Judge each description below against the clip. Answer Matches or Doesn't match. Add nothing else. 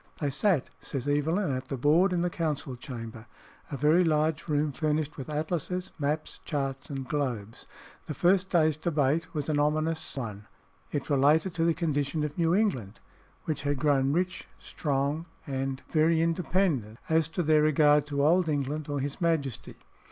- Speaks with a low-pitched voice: Doesn't match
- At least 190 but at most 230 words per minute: Doesn't match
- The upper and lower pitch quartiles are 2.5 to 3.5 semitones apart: Matches